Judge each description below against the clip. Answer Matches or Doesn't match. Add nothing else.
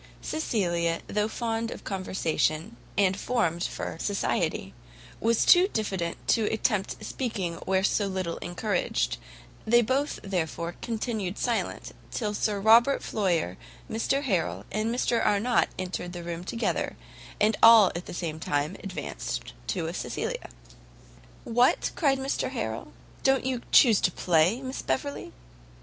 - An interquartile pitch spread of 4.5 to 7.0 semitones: Matches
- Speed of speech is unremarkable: Doesn't match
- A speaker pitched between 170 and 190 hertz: Doesn't match